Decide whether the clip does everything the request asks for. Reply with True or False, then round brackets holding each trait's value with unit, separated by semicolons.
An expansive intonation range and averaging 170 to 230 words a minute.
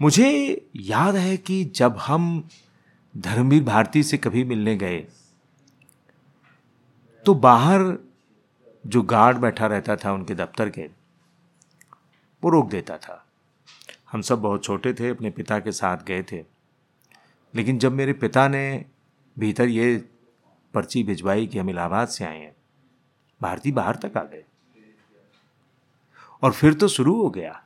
False (6.4 semitones; 135 wpm)